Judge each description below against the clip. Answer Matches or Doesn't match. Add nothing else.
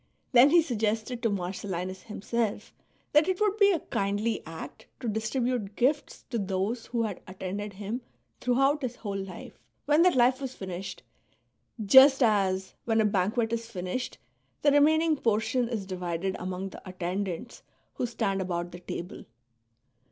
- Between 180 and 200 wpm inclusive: Doesn't match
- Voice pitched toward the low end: Doesn't match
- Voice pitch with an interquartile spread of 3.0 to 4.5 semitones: Doesn't match